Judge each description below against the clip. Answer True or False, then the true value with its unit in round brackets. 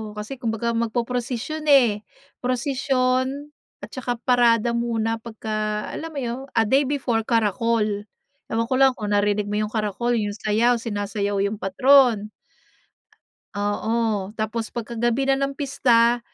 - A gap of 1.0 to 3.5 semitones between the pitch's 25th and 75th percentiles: True (3.0 semitones)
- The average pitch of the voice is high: True (230 Hz)